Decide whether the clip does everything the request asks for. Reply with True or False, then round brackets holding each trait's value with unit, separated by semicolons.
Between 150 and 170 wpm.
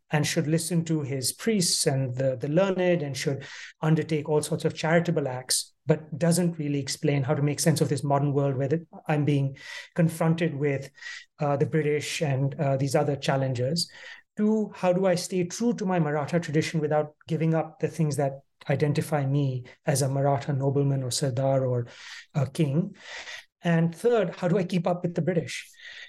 False (185 wpm)